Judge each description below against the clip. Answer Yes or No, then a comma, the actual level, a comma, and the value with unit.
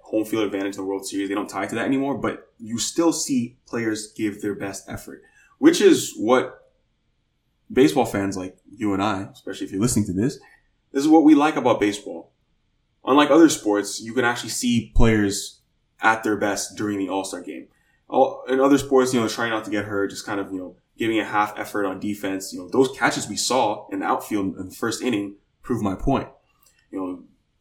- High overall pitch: No, low, 105 Hz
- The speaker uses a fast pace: Yes, fast, 215 wpm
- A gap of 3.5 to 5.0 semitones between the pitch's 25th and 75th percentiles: Yes, average, 3.9 semitones